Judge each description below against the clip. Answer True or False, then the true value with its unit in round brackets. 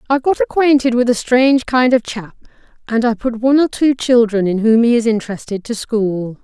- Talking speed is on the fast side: True (215 wpm)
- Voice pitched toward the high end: True (240 Hz)